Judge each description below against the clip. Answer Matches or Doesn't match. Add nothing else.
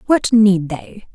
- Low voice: Doesn't match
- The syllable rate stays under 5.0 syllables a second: Matches